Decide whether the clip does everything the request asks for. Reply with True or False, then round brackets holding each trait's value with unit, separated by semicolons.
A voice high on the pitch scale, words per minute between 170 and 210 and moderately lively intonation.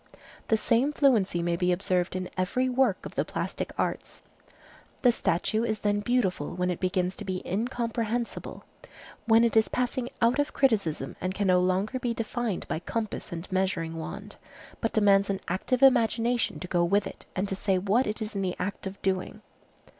True (205 Hz; 185 wpm; 4.2 semitones)